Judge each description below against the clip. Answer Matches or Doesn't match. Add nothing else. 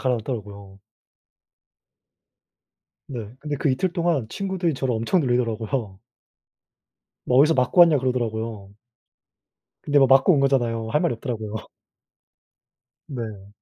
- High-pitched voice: Doesn't match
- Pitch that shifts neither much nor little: Matches